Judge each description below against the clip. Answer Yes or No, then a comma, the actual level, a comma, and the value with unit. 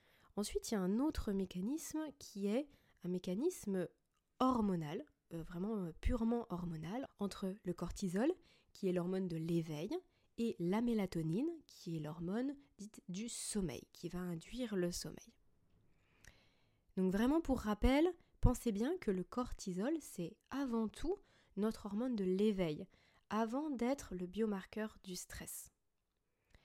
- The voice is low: No, high, 205 Hz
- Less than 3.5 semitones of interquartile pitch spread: No, wide, 5.4 semitones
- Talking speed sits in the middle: No, slow, 135 wpm